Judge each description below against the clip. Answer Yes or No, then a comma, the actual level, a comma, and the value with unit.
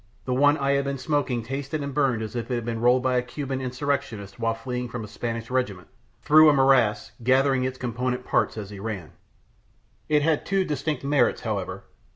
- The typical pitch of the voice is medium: No, low, 130 Hz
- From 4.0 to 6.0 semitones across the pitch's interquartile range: No, average, 3.2 semitones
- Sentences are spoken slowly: No, average, 200 wpm